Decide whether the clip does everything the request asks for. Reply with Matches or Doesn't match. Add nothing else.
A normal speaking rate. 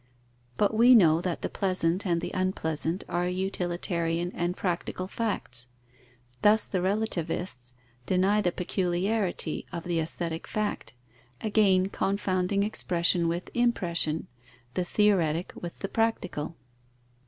Doesn't match